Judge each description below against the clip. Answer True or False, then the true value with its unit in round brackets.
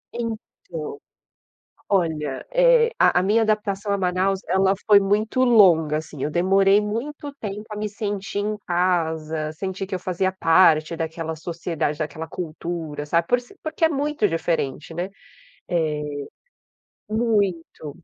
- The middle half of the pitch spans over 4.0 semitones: True (4.6 semitones)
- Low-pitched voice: False (190 Hz)